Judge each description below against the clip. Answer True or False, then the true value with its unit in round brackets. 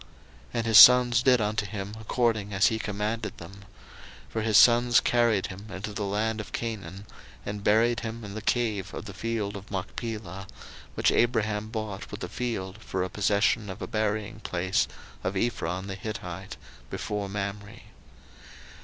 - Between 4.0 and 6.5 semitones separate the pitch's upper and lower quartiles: False (2.4 semitones)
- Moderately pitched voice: False (105 Hz)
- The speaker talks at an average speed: True (165 wpm)